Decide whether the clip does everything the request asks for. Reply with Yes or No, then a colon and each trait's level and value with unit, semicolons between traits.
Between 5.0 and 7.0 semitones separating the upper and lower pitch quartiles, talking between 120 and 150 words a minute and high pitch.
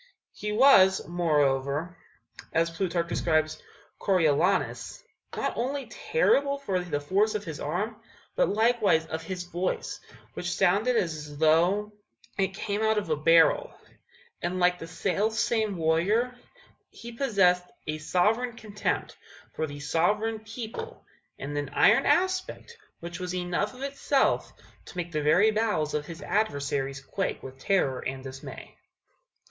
No: wide, 5.4 semitones; average, 140 wpm; medium, 180 Hz